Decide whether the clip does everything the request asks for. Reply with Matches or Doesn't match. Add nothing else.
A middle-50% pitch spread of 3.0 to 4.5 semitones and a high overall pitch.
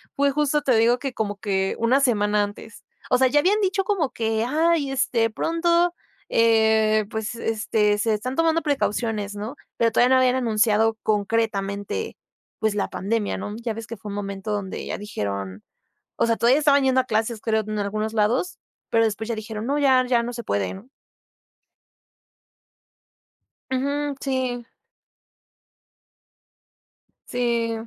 Matches